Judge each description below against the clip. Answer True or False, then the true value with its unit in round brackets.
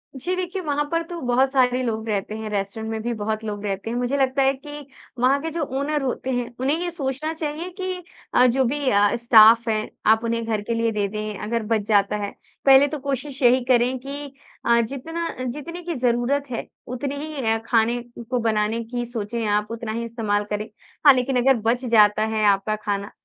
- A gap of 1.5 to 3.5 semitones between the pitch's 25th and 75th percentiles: False (4.0 semitones)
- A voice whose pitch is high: True (240 Hz)